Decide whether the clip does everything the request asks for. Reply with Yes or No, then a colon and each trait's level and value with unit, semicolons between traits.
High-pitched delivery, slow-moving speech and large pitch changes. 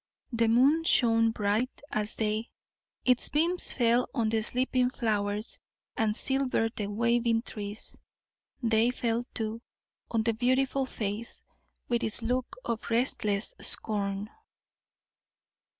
No: high, 230 Hz; slow, 120 wpm; narrow, 2.5 semitones